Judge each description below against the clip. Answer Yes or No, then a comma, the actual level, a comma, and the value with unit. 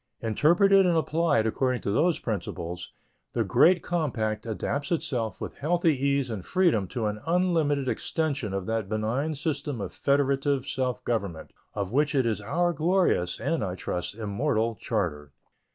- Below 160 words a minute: Yes, average, 150 wpm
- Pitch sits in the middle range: No, low, 130 Hz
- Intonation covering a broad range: Yes, wide, 6.7 semitones